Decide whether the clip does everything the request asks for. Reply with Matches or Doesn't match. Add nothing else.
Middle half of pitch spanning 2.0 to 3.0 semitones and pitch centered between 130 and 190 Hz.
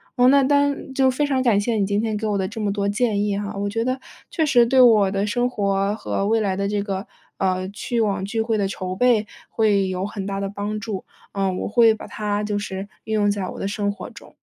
Doesn't match